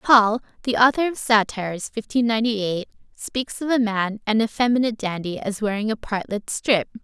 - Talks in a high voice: Yes, high, 220 Hz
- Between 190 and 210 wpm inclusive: No, average, 170 wpm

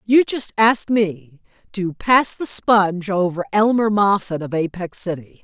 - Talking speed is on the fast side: No, average, 155 wpm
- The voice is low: No, high, 195 Hz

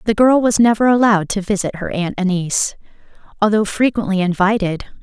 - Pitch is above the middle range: Yes, high, 205 Hz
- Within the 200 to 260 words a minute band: No, average, 155 wpm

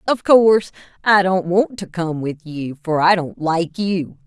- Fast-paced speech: No, average, 195 wpm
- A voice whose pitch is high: No, medium, 180 Hz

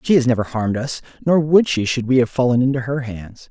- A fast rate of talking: Yes, fast, 255 wpm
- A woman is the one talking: No, male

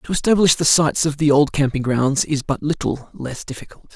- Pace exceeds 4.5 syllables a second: Yes, 5.5 syllables/s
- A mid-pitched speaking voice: Yes, medium, 145 Hz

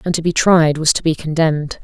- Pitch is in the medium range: Yes, medium, 160 Hz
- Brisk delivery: Yes, fast, 260 wpm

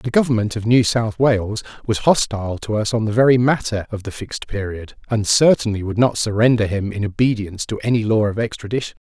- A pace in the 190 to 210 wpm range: Yes, fast, 205 wpm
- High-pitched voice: No, low, 110 Hz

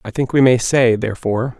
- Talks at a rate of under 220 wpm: No, fast, 225 wpm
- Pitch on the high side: No, low, 120 Hz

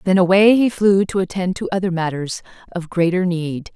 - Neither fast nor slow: Yes, average, 190 wpm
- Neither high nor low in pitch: Yes, medium, 180 Hz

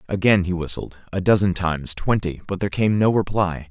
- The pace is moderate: Yes, average, 195 wpm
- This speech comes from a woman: No, male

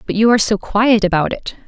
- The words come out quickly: Yes, fast, 250 wpm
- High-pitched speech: Yes, high, 210 Hz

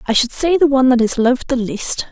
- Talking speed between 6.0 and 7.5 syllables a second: Yes, 6.4 syllables/s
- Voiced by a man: No, female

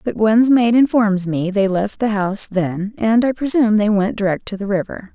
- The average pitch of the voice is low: No, high, 210 Hz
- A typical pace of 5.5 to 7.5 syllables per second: No, 5.0 syllables/s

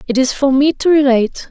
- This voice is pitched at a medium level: No, very high, 270 Hz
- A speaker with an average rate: No, fast, 240 wpm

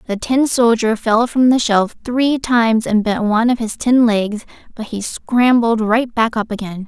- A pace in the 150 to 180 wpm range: No, average, 200 wpm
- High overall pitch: Yes, high, 230 Hz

